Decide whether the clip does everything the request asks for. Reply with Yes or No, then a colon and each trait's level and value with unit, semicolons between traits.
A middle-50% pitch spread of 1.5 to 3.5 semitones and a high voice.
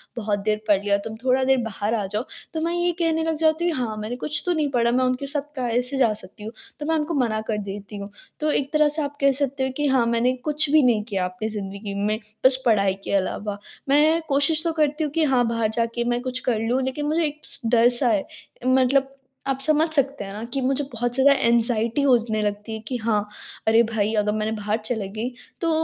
No: average, 4.7 semitones; high, 245 Hz